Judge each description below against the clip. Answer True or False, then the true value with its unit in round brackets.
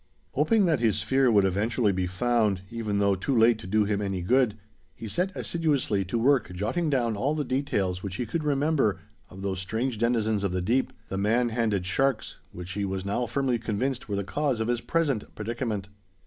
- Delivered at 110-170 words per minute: False (205 wpm)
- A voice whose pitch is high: False (110 Hz)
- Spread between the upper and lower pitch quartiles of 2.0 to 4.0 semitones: False (4.8 semitones)